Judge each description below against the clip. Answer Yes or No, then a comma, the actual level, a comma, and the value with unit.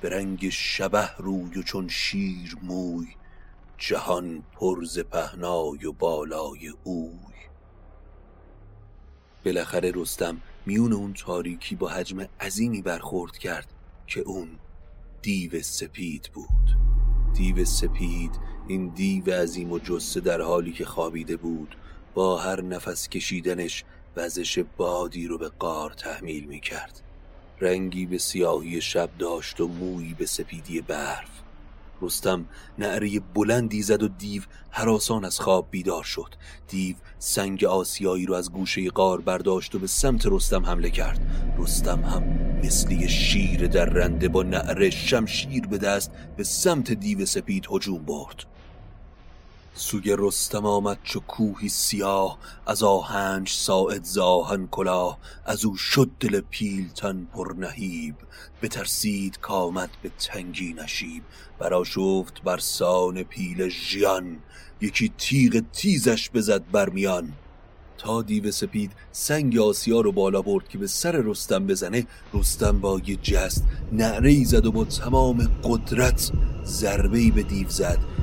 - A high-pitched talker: No, very low, 95 Hz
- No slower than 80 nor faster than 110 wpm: No, average, 130 wpm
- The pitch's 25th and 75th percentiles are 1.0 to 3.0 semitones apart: No, average, 3.4 semitones